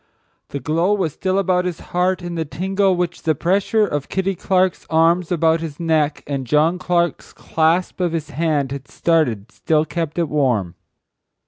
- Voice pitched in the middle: Yes, medium, 165 Hz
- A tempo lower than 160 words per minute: No, average, 175 wpm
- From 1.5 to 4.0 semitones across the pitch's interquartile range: Yes, average, 3.1 semitones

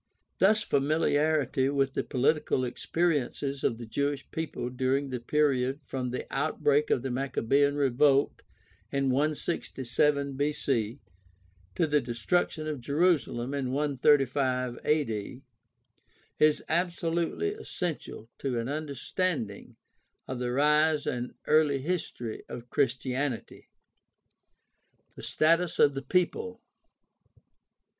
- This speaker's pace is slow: Yes, slow, 105 wpm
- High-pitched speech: No, medium, 140 Hz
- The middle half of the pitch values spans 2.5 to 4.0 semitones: Yes, average, 3.2 semitones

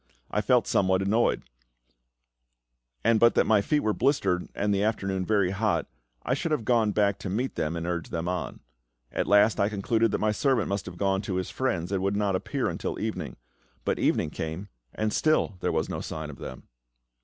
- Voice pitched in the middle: No, low, 100 Hz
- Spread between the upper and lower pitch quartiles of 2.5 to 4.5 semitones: Yes, average, 3.0 semitones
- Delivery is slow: No, average, 200 wpm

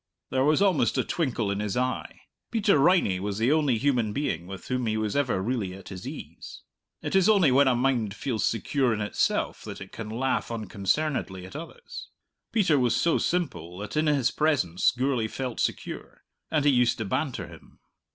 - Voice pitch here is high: No, low, 125 Hz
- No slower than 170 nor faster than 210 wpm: Yes, average, 190 wpm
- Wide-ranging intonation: Yes, wide, 5.9 semitones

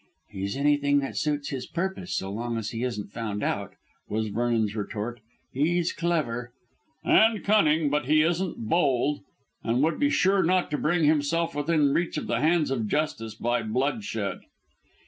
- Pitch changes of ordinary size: No, wide, 6.3 semitones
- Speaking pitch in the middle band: Yes, medium, 145 Hz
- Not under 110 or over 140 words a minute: No, average, 165 wpm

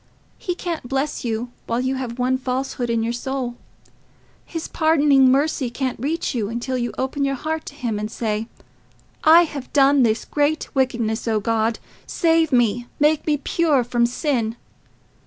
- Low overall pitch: No, very high, 260 Hz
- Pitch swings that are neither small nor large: Yes, average, 3.7 semitones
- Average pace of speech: Yes, average, 165 wpm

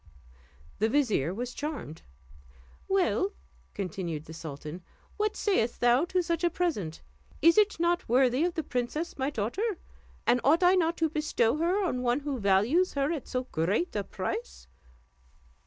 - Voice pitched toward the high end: Yes, very high, 275 Hz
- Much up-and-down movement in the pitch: Yes, wide, 8.1 semitones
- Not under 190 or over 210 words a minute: No, average, 155 wpm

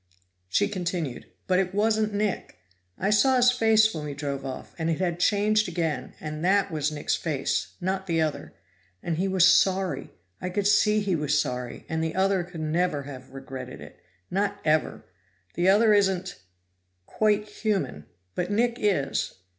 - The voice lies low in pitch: No, medium, 180 Hz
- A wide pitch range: No, average, 5.0 semitones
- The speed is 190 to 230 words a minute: No, average, 170 wpm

